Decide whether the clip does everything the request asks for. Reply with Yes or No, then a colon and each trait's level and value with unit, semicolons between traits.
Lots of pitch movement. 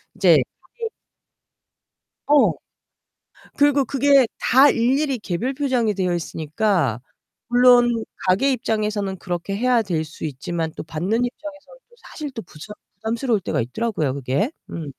Yes: wide, 7.1 semitones